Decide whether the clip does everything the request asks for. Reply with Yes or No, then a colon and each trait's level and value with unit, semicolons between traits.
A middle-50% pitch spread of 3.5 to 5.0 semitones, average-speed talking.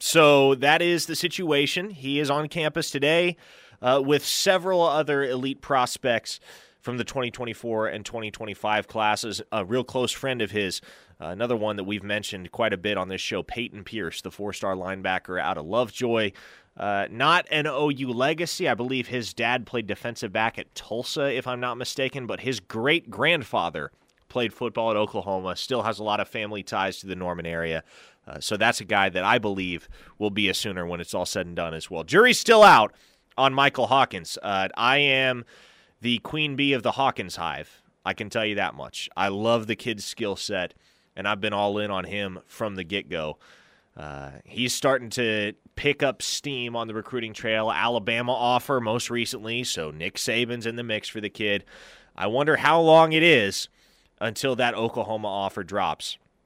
Yes: average, 4.4 semitones; average, 190 wpm